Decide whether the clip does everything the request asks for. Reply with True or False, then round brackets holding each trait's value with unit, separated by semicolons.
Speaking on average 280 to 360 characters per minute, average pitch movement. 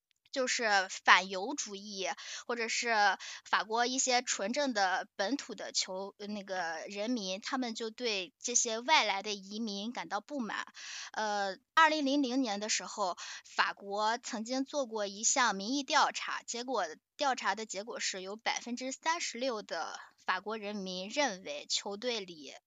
False (225 characters per minute; 4.6 semitones)